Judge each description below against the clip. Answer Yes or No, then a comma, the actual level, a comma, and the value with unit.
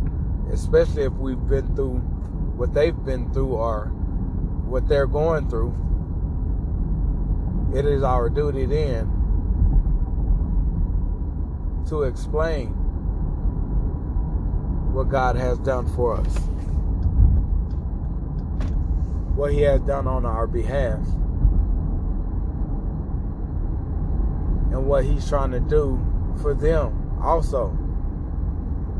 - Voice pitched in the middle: No, very low, 80 Hz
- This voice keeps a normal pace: No, slow, 90 wpm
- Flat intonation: Yes, narrow, 2.2 semitones